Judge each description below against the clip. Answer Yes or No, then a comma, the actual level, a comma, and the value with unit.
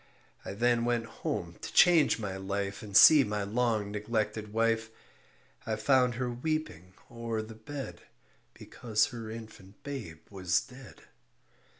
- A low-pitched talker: Yes, low, 110 Hz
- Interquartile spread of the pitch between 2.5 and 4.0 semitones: Yes, average, 2.9 semitones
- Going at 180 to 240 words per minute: No, slow, 135 wpm